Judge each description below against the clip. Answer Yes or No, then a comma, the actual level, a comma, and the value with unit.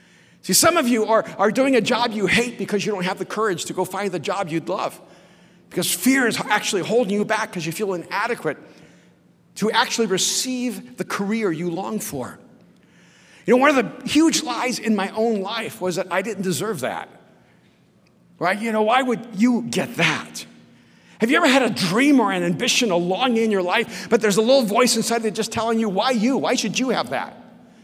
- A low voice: No, high, 215 Hz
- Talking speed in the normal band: No, fast, 215 wpm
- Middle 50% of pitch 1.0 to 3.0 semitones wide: No, average, 4.1 semitones